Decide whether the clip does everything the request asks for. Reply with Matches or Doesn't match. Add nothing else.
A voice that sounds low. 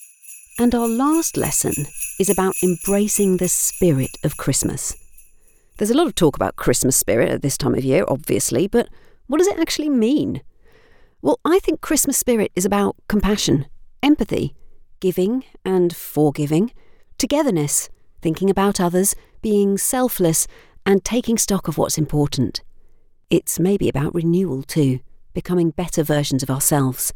Doesn't match